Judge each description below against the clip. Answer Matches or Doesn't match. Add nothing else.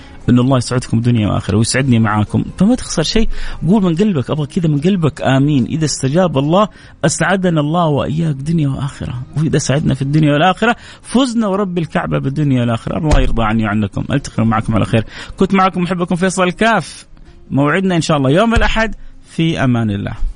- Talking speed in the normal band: Doesn't match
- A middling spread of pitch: Doesn't match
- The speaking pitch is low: Doesn't match